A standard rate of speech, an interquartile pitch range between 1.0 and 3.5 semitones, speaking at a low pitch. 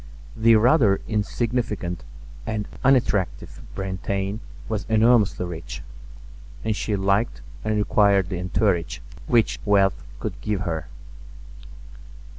No: slow, 100 wpm; average, 2.9 semitones; low, 105 Hz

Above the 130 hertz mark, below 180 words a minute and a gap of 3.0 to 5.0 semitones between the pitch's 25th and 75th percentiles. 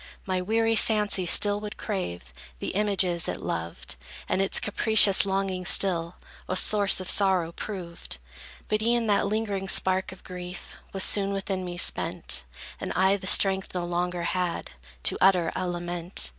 No: high, 190 Hz; average, 155 wpm; narrow, 2.4 semitones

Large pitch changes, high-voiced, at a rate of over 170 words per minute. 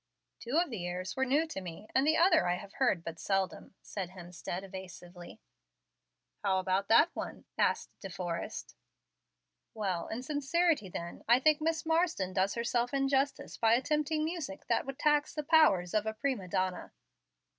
No: wide, 7.9 semitones; high, 225 Hz; average, 165 wpm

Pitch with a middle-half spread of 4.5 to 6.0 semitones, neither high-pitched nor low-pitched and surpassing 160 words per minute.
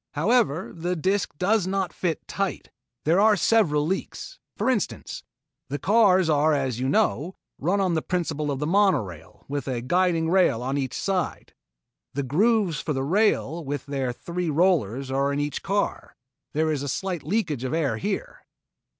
Yes: average, 5.3 semitones; medium, 160 Hz; average, 170 wpm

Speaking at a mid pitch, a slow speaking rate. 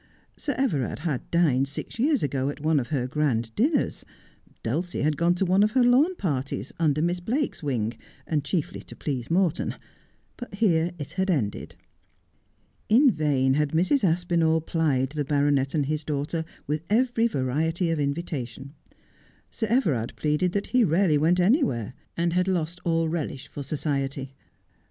No: medium, 160 Hz; average, 160 wpm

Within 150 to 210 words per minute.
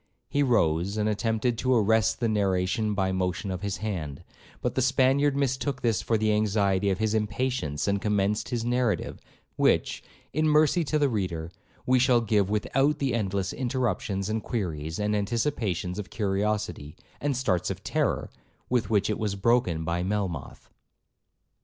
Yes: average, 165 wpm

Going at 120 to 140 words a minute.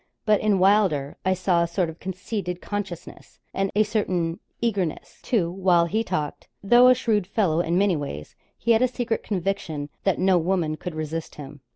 No: average, 185 wpm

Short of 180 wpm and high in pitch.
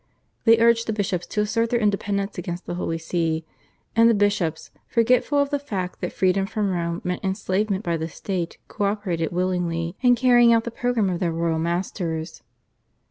No: average, 185 wpm; high, 195 Hz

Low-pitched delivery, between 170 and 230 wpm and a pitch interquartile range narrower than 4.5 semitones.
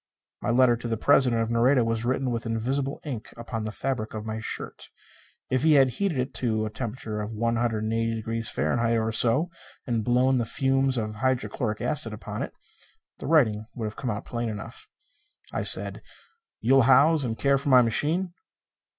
Yes: low, 120 Hz; average, 175 wpm; average, 3.0 semitones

